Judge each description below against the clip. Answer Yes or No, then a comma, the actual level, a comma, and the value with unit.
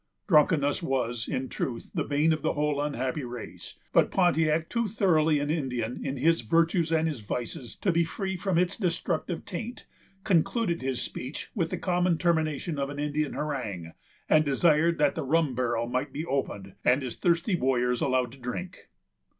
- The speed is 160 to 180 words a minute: Yes, average, 175 wpm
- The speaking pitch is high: No, medium, 150 Hz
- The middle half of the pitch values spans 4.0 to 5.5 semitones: Yes, average, 4.6 semitones